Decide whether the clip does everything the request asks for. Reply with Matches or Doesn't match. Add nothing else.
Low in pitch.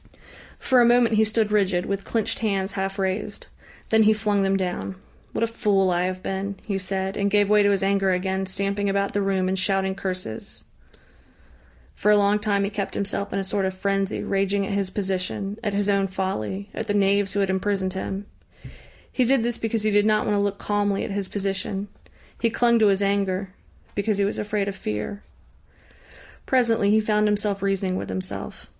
Doesn't match